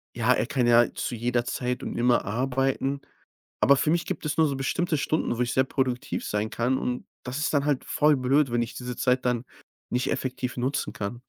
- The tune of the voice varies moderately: No, narrow, 2.2 semitones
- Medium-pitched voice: No, low, 125 Hz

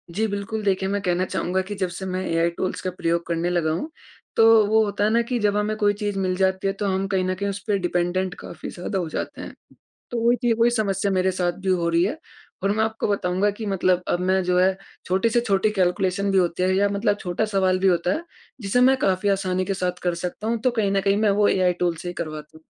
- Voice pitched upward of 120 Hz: Yes, high, 190 Hz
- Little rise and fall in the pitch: Yes, narrow, 2.3 semitones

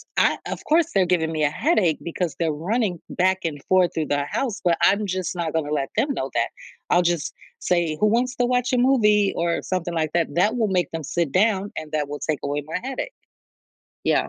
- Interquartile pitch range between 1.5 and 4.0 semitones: No, average, 5.0 semitones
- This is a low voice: No, medium, 175 Hz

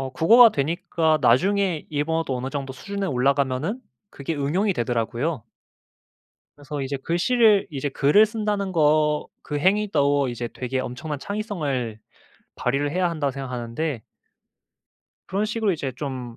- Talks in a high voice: No, medium, 145 Hz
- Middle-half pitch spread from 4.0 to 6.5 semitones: Yes, wide, 6.0 semitones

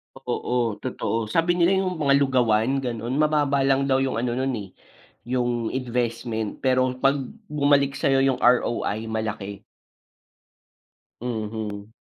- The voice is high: No, low, 125 Hz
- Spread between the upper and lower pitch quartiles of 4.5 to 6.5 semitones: No, average, 3.2 semitones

